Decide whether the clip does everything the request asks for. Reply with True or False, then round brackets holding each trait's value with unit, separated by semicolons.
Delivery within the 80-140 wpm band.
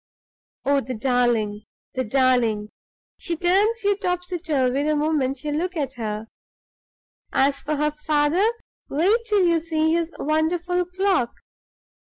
True (135 wpm)